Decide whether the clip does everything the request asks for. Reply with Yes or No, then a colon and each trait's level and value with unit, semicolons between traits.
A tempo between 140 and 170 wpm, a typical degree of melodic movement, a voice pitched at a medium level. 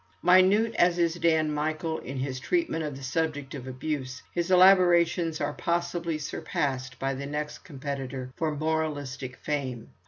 Yes: average, 150 wpm; average, 3.9 semitones; medium, 150 Hz